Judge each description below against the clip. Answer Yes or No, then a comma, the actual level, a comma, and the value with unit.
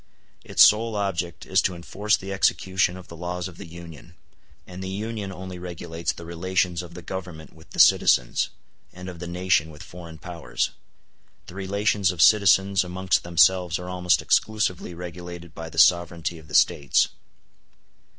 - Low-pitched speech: Yes, very low, 90 Hz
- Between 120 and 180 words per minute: Yes, average, 165 wpm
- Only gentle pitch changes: Yes, narrow, 1.8 semitones